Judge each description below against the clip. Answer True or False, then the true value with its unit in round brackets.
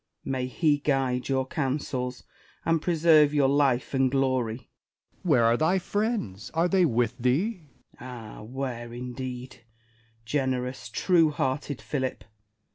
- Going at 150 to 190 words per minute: False (135 wpm)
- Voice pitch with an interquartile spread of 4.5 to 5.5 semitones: False (3.3 semitones)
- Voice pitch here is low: True (130 Hz)